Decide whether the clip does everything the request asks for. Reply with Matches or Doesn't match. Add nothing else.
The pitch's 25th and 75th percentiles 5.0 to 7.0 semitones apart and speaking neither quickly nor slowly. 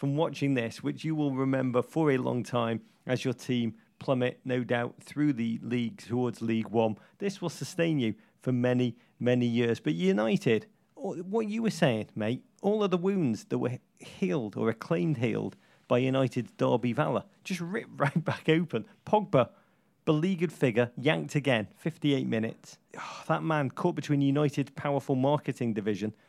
Matches